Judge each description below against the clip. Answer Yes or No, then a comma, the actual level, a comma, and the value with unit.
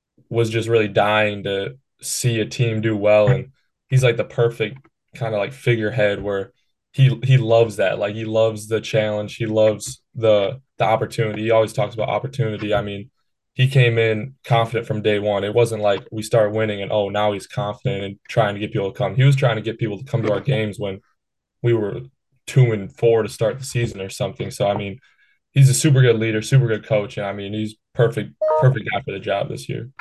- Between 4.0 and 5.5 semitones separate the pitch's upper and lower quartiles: No, average, 3.3 semitones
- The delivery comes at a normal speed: No, fast, 225 wpm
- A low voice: Yes, low, 110 Hz